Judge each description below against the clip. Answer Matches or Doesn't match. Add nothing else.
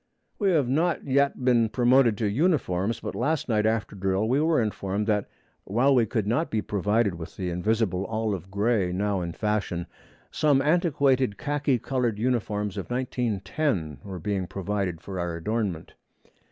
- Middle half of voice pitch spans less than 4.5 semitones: Doesn't match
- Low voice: Matches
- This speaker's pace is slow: Doesn't match